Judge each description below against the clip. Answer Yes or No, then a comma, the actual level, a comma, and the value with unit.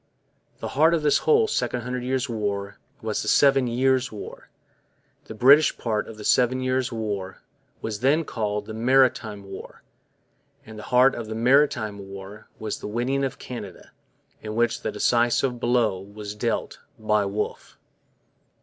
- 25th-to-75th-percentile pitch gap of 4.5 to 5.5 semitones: No, average, 3.5 semitones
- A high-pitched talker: No, low, 115 Hz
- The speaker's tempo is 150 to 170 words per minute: Yes, average, 160 wpm